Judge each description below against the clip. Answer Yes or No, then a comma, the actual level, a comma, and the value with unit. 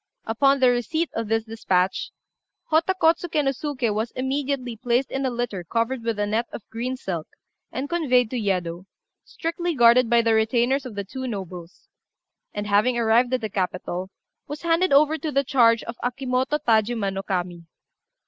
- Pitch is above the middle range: Yes, high, 240 Hz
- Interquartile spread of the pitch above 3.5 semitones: Yes, average, 4.3 semitones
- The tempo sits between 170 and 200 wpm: Yes, average, 175 wpm